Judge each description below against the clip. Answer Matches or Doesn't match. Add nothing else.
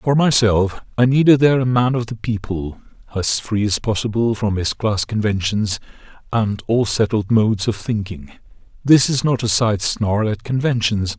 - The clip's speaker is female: Doesn't match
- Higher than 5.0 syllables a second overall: Doesn't match